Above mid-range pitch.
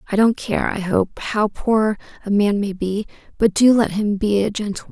Yes: high, 210 Hz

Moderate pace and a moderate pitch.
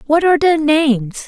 No: average, 190 wpm; very high, 290 Hz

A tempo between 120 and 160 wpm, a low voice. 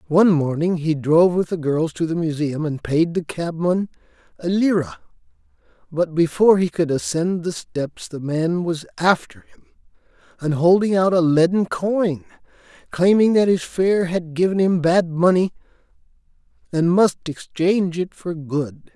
No: average, 155 wpm; medium, 170 Hz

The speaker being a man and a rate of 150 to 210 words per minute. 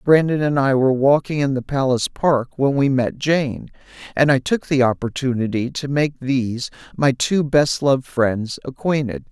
Yes: male; average, 175 wpm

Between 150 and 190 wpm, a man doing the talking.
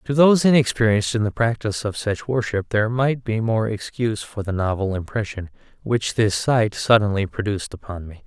Yes: average, 180 wpm; male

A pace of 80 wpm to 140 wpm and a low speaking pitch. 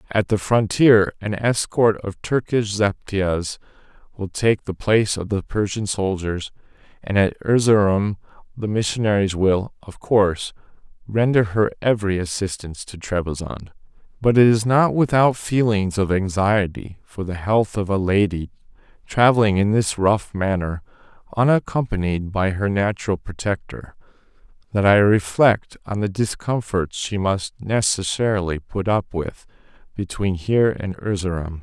Yes: slow, 135 wpm; low, 100 Hz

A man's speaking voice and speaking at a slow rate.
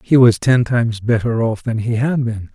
No: male; fast, 235 wpm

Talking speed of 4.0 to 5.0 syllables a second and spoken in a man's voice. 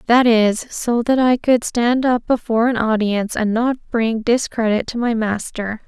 No: 4.5 syllables/s; female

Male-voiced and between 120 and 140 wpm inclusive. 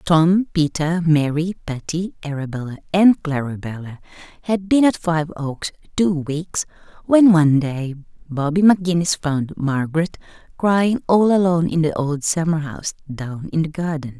No: female; slow, 135 wpm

